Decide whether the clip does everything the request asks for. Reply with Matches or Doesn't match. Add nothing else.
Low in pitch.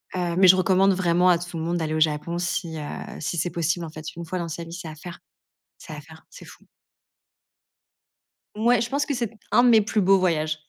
Doesn't match